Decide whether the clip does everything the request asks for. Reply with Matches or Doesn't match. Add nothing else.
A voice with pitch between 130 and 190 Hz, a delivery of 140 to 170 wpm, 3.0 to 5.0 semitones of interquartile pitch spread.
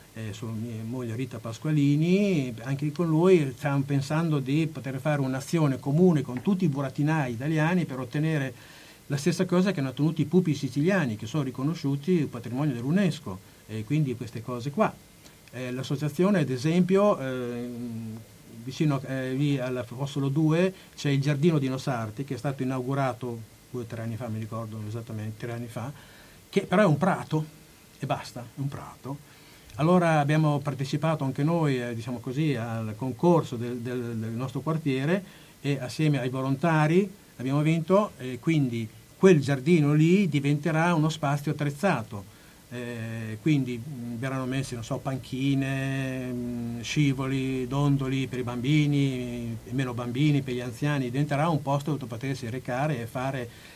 Matches